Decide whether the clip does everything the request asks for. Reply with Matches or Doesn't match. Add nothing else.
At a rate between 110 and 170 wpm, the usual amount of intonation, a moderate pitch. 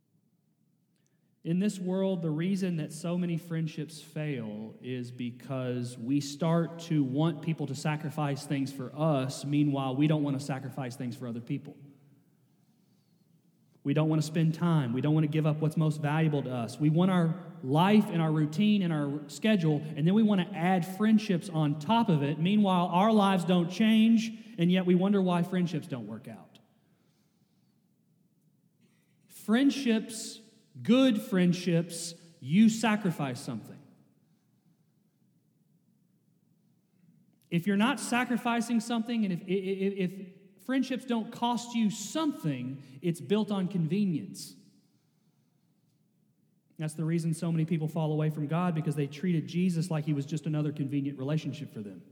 Matches